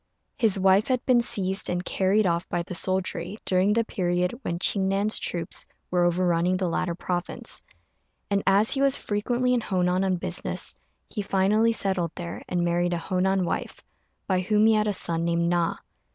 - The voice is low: No, medium, 185 Hz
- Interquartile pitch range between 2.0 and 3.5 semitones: Yes, average, 2.8 semitones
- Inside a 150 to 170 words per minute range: No, average, 180 wpm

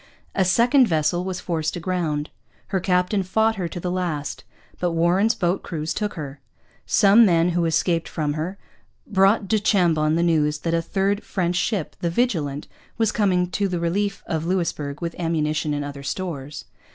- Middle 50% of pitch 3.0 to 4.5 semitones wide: Yes, average, 3.5 semitones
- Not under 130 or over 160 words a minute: No, average, 175 wpm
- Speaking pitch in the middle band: Yes, medium, 175 Hz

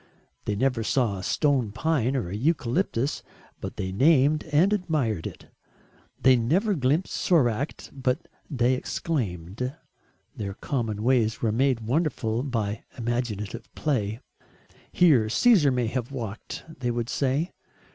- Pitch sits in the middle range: No, low, 125 Hz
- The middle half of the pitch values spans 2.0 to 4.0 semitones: No, average, 4.6 semitones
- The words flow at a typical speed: No, slow, 130 wpm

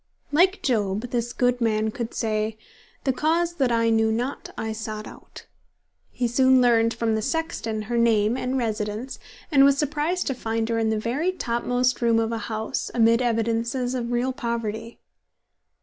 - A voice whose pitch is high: Yes, high, 235 Hz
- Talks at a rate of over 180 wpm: No, average, 170 wpm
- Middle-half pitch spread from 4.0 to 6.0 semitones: No, narrow, 2.4 semitones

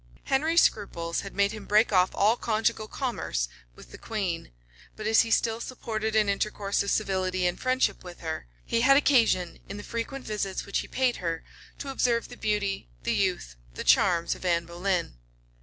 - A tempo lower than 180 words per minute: No, average, 185 wpm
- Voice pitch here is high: Yes, high, 205 Hz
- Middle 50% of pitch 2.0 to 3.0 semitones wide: No, average, 4.3 semitones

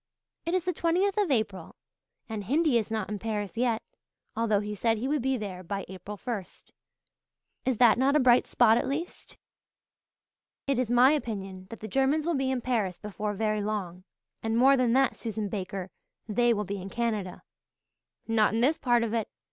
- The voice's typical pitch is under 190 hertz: No, high, 225 Hz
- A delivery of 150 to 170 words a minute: No, average, 190 wpm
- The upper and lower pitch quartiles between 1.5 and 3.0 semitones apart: No, average, 4.0 semitones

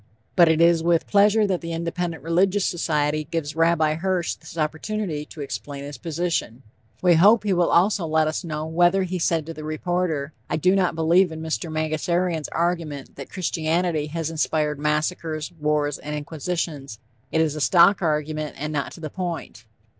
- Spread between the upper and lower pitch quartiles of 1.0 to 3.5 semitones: Yes, narrow, 2.5 semitones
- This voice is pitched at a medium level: Yes, medium, 160 Hz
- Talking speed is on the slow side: No, average, 175 wpm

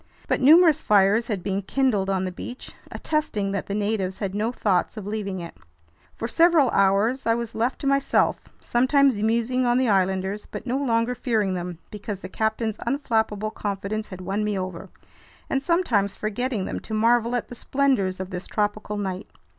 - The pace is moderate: Yes, average, 175 wpm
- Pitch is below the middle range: No, high, 215 Hz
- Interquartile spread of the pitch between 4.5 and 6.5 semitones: No, average, 3.9 semitones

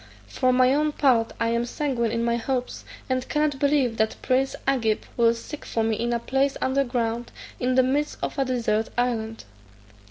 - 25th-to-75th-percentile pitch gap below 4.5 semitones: Yes, average, 2.7 semitones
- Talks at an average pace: Yes, average, 190 wpm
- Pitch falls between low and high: No, very high, 250 Hz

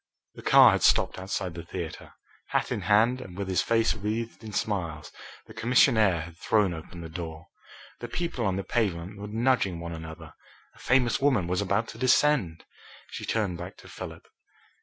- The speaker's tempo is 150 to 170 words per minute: No, average, 180 wpm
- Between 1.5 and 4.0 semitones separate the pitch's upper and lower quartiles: No, average, 5.1 semitones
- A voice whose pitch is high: No, low, 100 Hz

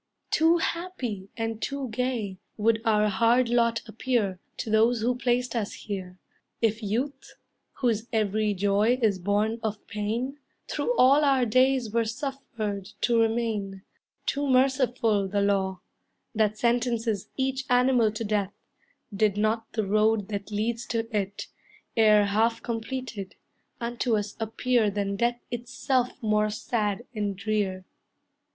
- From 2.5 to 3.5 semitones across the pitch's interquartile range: Yes, average, 2.9 semitones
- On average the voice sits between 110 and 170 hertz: No, high, 225 Hz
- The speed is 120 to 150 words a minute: Yes, slow, 135 wpm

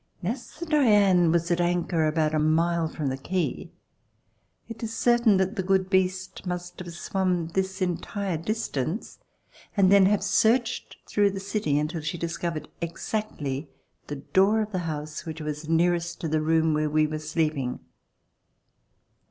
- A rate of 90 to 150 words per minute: No, average, 160 wpm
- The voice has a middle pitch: Yes, medium, 175 Hz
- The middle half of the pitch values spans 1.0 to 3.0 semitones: No, average, 3.8 semitones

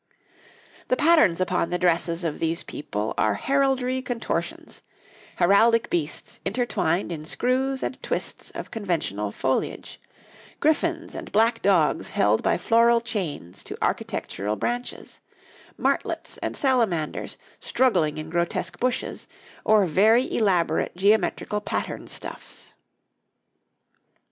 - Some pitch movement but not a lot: No, wide, 6.8 semitones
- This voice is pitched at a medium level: No, high, 195 Hz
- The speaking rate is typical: No, slow, 110 wpm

